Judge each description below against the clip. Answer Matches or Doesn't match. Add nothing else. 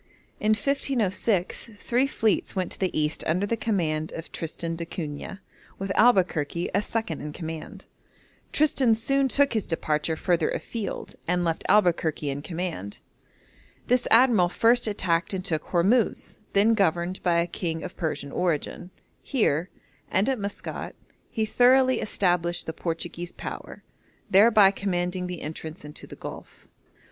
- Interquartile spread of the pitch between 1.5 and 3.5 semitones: Doesn't match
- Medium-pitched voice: Matches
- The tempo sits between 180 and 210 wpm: Doesn't match